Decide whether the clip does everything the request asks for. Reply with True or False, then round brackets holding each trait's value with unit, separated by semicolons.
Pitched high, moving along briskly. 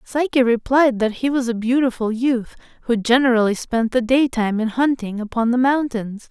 False (240 Hz; 170 wpm)